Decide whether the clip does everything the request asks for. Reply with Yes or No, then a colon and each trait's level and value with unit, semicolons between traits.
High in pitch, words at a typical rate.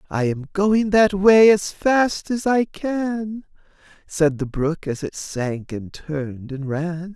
No: medium, 175 Hz; average, 170 wpm